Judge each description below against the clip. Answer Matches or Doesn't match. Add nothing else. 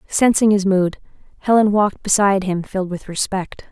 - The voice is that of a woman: Matches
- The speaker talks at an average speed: Matches